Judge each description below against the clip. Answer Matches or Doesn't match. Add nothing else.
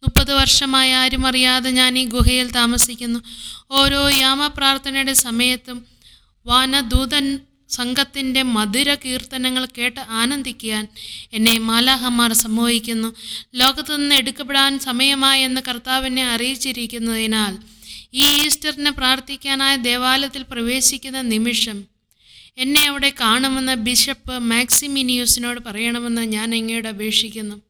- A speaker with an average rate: Matches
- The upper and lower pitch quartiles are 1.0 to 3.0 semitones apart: Matches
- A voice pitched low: Doesn't match